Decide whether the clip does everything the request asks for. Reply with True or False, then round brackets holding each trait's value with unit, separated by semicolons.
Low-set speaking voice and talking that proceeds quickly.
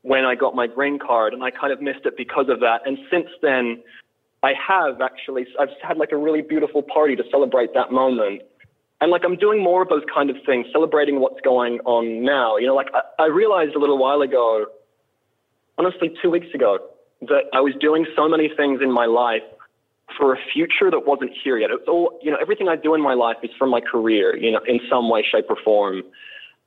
False (145 Hz; 225 wpm)